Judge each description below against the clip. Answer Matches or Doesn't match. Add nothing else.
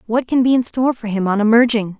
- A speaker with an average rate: Doesn't match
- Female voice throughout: Matches